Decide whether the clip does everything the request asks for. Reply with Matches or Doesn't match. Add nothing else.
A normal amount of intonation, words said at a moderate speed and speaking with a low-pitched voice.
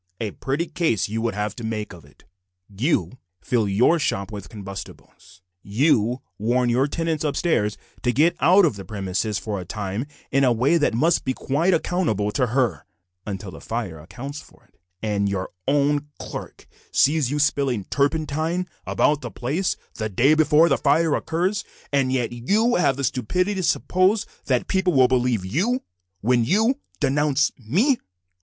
Doesn't match